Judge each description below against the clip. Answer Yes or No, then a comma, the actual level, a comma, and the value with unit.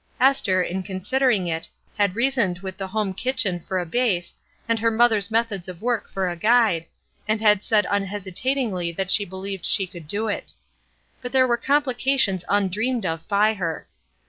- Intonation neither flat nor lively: Yes, average, 4.0 semitones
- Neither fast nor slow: Yes, average, 175 wpm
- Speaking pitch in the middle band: No, high, 205 Hz